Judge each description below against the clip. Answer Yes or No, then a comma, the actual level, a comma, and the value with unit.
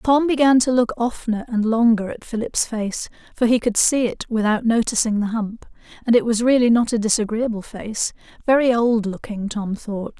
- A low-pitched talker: No, high, 230 Hz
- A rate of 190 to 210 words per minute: No, average, 180 wpm